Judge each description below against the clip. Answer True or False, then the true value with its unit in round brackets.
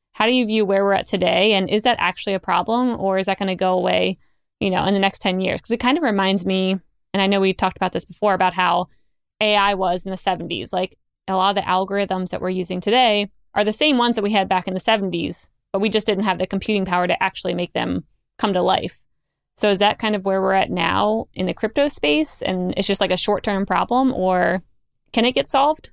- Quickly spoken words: True (255 wpm)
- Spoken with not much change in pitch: True (2.2 semitones)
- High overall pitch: True (195 Hz)